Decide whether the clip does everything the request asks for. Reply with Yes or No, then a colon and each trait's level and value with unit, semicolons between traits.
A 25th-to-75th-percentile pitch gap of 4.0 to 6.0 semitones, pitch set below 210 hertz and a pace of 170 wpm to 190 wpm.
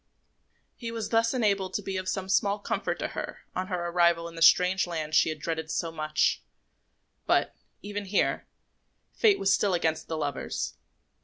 No: average, 3.6 semitones; medium, 185 Hz; average, 175 wpm